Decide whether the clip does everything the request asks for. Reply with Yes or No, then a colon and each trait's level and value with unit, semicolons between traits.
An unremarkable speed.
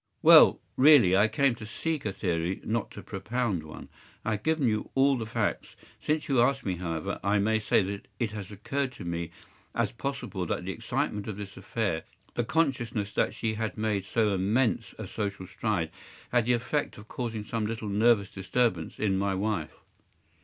Yes: average, 190 wpm